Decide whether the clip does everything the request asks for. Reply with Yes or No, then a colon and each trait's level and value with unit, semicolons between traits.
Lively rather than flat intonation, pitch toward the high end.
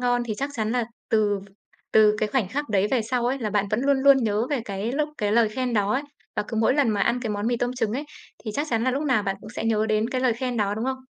No: average, 3.3 semitones; high, 230 Hz